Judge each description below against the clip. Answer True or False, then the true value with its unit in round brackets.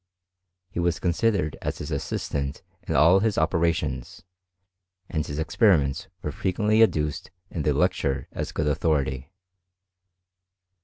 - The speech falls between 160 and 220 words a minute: False (135 wpm)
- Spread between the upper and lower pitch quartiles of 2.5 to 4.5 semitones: True (4.0 semitones)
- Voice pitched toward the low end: True (80 Hz)